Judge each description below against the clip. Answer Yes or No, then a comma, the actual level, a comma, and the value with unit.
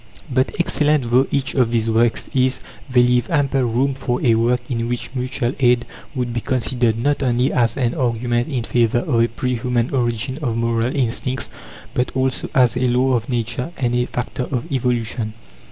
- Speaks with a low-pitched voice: Yes, low, 125 Hz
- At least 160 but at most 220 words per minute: Yes, average, 185 wpm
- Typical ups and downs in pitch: No, narrow, 1.8 semitones